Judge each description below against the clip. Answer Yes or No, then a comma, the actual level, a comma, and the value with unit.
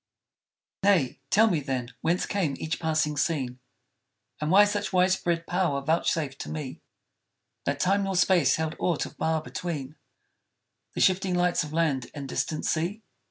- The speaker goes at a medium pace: Yes, average, 155 wpm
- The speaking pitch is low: No, medium, 160 Hz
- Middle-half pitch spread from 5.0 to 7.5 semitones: No, average, 3.7 semitones